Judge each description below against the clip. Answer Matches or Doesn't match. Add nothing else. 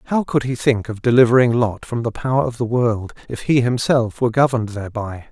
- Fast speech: Matches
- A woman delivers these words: Doesn't match